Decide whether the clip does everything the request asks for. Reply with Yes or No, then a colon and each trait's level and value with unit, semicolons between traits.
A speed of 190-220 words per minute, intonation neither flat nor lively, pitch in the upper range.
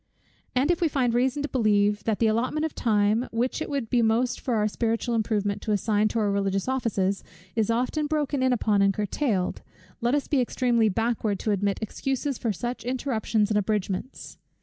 Yes: average, 195 wpm; average, 3.6 semitones; high, 230 Hz